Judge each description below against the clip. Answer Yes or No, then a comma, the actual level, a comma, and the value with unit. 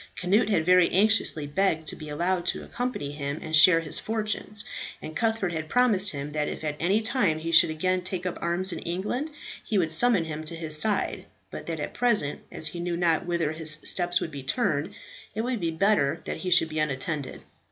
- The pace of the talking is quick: Yes, fast, 215 wpm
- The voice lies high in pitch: No, medium, 170 Hz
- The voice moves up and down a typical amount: Yes, average, 4.2 semitones